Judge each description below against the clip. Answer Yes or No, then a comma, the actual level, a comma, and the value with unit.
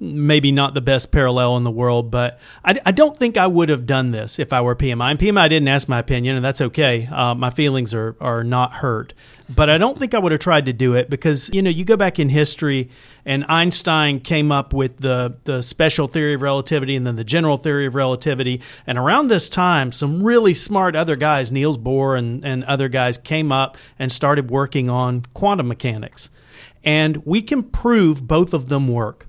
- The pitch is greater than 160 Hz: No, medium, 140 Hz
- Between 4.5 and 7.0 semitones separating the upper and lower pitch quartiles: No, average, 3.8 semitones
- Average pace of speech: No, fast, 215 wpm